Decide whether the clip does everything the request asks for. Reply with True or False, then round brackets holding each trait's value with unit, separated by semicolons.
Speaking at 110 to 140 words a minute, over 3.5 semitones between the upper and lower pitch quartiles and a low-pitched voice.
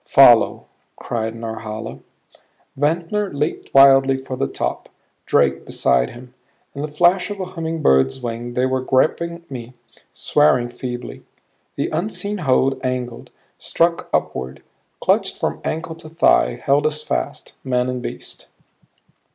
True (135 wpm; 5.1 semitones; 130 Hz)